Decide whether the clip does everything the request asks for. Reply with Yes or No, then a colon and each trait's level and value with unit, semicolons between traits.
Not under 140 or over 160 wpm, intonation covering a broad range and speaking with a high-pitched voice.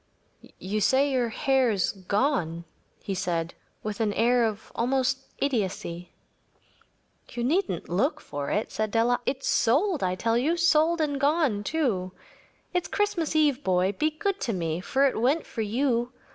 Yes: average, 155 wpm; wide, 6.2 semitones; high, 240 Hz